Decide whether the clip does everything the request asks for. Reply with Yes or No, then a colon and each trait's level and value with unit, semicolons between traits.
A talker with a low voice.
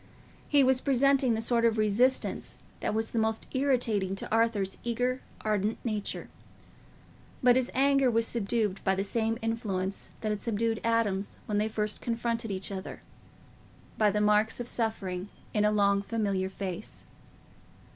No: high, 220 Hz